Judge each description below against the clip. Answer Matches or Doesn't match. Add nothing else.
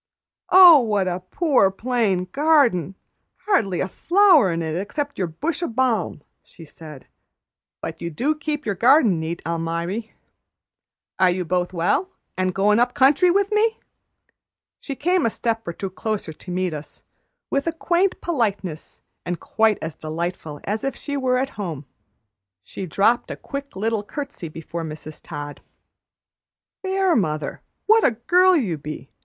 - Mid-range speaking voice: Doesn't match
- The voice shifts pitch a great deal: Matches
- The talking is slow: Doesn't match